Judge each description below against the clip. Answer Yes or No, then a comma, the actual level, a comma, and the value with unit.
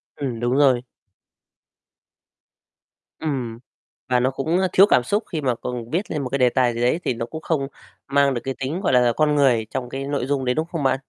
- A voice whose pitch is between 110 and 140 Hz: Yes, low, 135 Hz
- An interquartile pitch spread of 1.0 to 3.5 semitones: Yes, average, 3.1 semitones